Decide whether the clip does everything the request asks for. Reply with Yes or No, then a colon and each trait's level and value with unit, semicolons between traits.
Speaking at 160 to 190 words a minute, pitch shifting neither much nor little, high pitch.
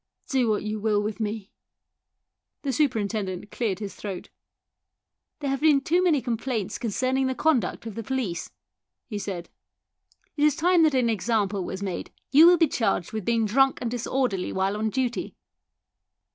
Yes: average, 175 wpm; average, 4.6 semitones; high, 230 Hz